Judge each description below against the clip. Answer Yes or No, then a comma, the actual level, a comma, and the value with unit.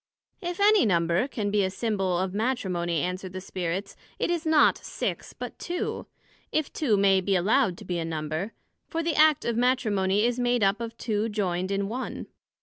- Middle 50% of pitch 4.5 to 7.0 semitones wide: Yes, average, 4.9 semitones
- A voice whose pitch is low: No, high, 205 Hz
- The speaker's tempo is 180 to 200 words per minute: Yes, average, 190 wpm